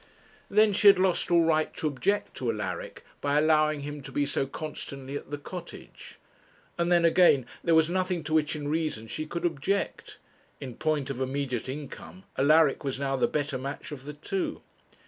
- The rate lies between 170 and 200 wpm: Yes, average, 185 wpm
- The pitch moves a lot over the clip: No, average, 3.5 semitones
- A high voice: No, medium, 150 Hz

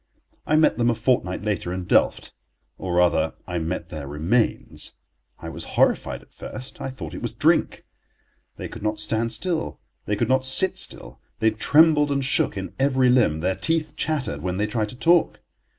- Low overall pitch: Yes, low, 110 Hz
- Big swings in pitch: Yes, wide, 6.6 semitones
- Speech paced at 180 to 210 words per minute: Yes, average, 185 wpm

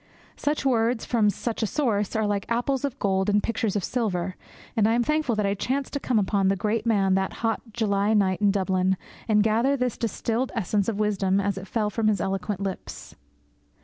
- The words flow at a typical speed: No, fast, 210 wpm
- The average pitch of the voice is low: No, high, 210 Hz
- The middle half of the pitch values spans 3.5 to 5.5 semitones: No, average, 2.9 semitones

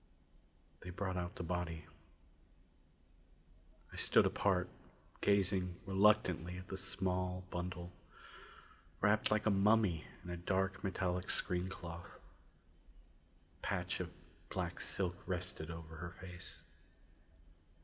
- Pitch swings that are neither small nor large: No, narrow, 1.6 semitones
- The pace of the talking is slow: Yes, slow, 110 wpm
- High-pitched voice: No, very low, 90 Hz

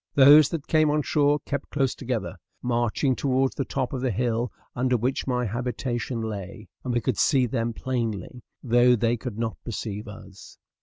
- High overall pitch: No, low, 125 Hz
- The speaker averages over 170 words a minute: Yes, average, 185 wpm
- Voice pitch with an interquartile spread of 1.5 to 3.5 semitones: Yes, average, 2.7 semitones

